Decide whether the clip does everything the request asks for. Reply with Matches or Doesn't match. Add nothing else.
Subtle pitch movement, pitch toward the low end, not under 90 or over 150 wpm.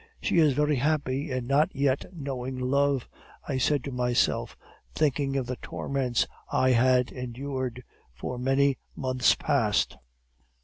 Matches